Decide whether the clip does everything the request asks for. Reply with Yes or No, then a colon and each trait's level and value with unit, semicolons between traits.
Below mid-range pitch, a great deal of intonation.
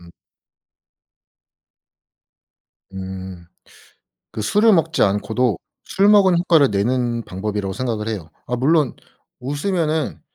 Yes: low, 125 Hz; wide, 8.2 semitones